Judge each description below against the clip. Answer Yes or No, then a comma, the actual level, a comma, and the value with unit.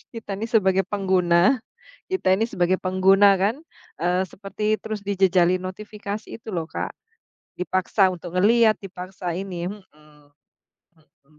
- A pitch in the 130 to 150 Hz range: No, high, 190 Hz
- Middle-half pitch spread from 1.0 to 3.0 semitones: Yes, narrow, 2.5 semitones